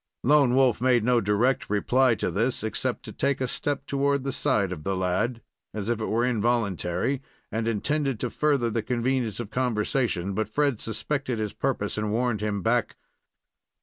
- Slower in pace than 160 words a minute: No, average, 180 wpm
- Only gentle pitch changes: No, average, 3.7 semitones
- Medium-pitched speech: No, low, 120 Hz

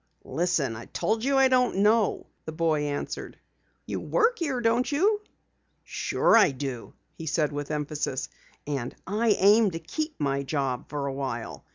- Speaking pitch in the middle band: Yes, medium, 160 Hz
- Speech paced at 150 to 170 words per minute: Yes, average, 160 wpm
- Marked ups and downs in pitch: Yes, wide, 8.6 semitones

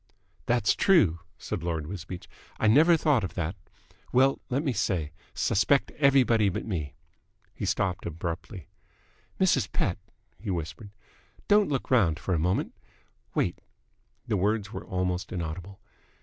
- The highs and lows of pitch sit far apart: Yes, wide, 6.2 semitones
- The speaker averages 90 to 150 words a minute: Yes, slow, 135 wpm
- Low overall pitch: Yes, very low, 95 Hz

